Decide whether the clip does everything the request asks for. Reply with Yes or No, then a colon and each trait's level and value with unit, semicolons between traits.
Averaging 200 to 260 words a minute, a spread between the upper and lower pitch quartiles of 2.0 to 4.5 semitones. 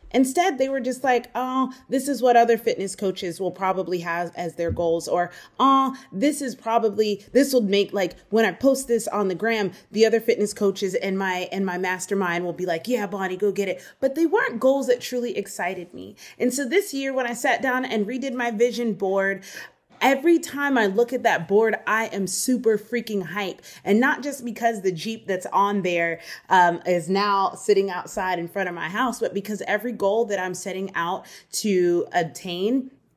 No: fast, 205 wpm; average, 4.9 semitones